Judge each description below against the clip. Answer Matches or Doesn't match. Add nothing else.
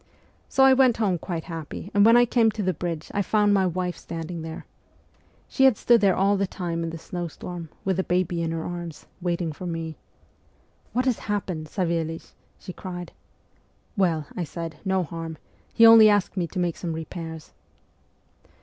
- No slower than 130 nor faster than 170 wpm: Doesn't match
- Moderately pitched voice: Matches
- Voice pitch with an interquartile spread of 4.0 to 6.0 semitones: Doesn't match